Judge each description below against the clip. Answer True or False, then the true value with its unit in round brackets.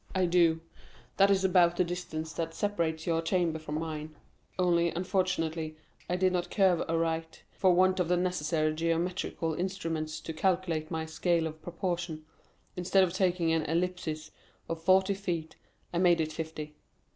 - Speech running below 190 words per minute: True (155 wpm)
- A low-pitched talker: False (170 Hz)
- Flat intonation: True (2.2 semitones)